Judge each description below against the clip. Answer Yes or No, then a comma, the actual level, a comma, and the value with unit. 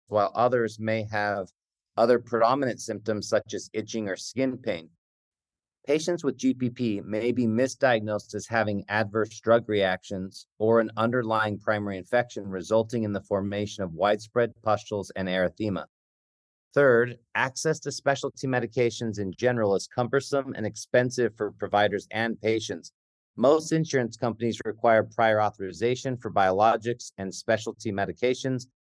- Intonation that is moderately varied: Yes, average, 3.1 semitones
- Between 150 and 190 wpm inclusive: No, slow, 135 wpm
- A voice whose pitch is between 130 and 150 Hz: No, low, 110 Hz